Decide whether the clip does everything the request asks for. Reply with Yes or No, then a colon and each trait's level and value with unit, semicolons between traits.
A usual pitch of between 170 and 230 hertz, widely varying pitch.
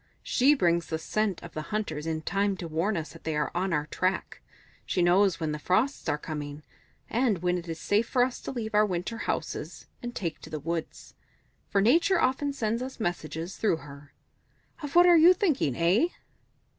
Yes: medium, 185 Hz; wide, 6.5 semitones